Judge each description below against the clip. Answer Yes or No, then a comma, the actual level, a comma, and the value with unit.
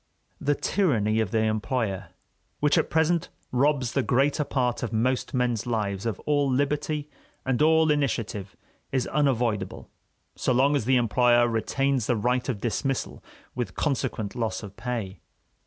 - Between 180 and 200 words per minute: No, average, 150 wpm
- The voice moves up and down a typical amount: Yes, average, 4.0 semitones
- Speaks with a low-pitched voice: Yes, low, 125 Hz